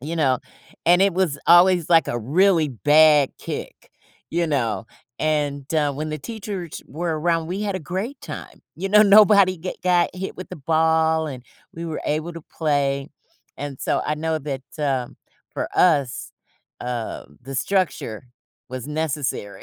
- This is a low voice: No, medium, 160 Hz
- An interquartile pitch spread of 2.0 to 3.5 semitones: No, average, 3.9 semitones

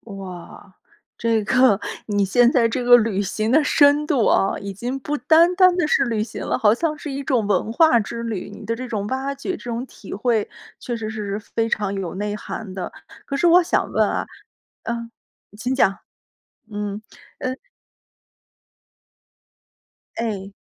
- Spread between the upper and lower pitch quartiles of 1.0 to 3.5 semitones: No, average, 4.4 semitones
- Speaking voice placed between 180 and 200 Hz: No, high, 230 Hz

